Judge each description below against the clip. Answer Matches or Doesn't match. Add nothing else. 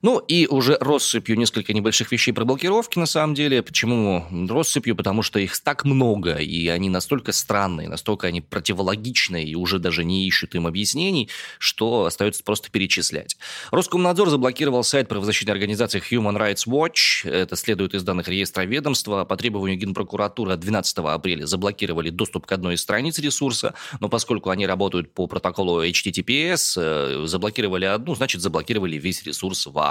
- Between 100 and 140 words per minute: Doesn't match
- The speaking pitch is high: Doesn't match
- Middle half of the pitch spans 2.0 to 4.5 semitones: Doesn't match